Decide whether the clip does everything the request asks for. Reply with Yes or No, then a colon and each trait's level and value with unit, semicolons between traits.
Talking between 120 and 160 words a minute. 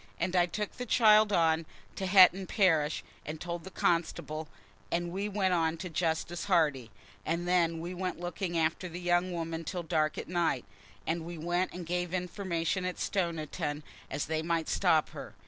No: average, 180 wpm